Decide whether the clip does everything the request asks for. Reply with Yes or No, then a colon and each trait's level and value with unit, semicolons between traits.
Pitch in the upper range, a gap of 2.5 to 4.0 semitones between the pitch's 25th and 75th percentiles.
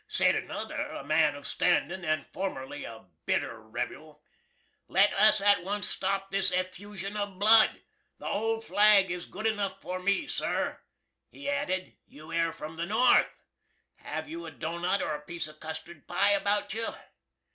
Yes: high, 195 Hz; average, 3.3 semitones